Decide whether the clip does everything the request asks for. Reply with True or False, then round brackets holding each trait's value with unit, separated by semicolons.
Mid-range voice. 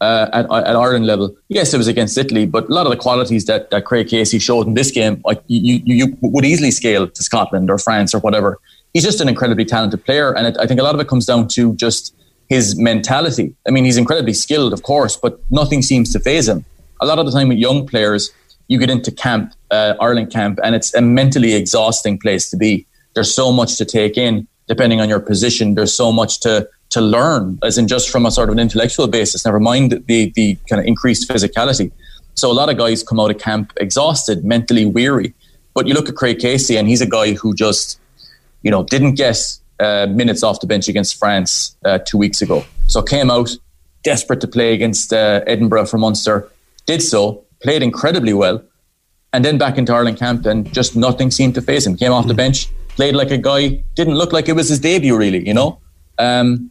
False (115 Hz)